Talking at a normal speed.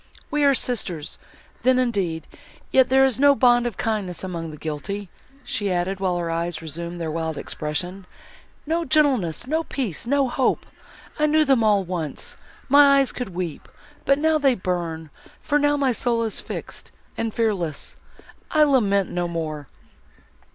Yes: average, 150 wpm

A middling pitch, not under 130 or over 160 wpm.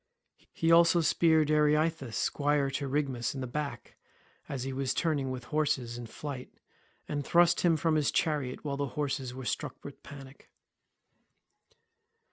Yes: medium, 145 Hz; average, 150 wpm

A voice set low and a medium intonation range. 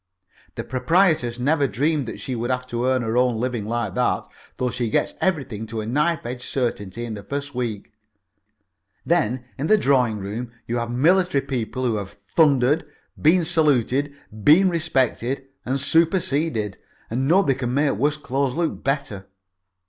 Yes: low, 130 Hz; average, 4.0 semitones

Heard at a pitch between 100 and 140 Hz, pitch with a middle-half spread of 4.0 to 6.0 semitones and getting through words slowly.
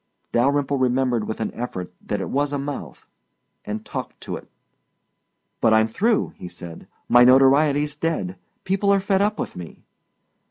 No: low, 135 Hz; average, 5.2 semitones; average, 160 wpm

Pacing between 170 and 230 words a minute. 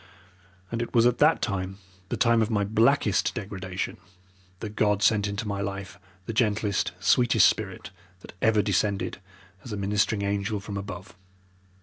No: average, 155 wpm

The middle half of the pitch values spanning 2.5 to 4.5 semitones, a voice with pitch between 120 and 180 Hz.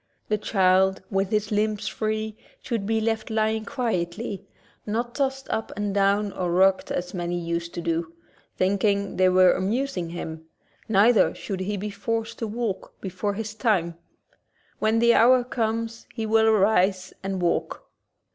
No: average, 3.0 semitones; high, 205 Hz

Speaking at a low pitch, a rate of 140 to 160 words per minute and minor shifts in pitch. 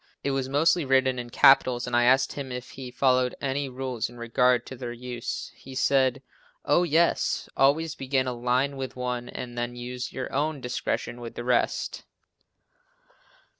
No: low, 130 Hz; average, 170 wpm; narrow, 1.7 semitones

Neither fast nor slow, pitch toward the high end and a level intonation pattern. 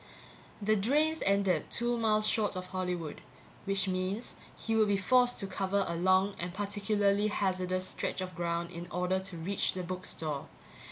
Yes: average, 170 wpm; high, 195 Hz; narrow, 2.2 semitones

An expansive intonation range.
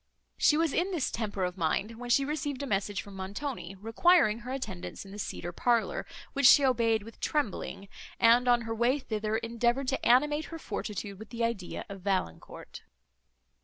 No: average, 4.9 semitones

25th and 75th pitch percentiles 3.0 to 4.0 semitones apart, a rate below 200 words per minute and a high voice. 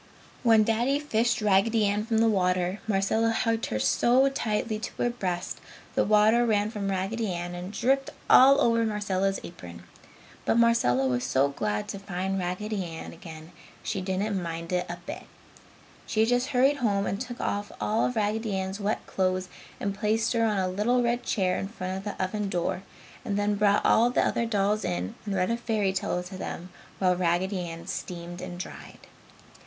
Yes: average, 3.6 semitones; average, 190 wpm; high, 200 Hz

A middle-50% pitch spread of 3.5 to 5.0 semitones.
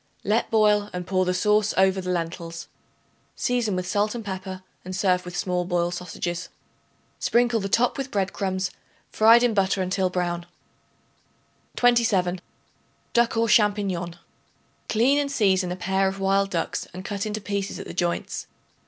No: average, 2.9 semitones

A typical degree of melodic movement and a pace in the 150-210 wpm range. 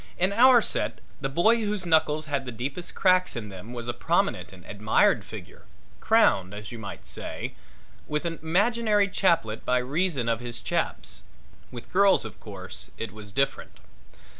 No: wide, 8.5 semitones; average, 165 wpm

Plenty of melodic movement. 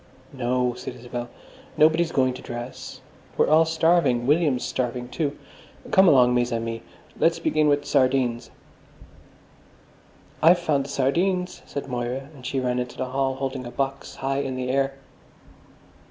No: average, 3.1 semitones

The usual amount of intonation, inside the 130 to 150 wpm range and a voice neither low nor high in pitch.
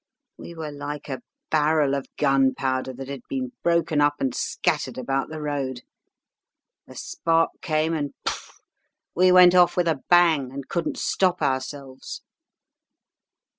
Yes: average, 3.4 semitones; average, 140 wpm; medium, 145 Hz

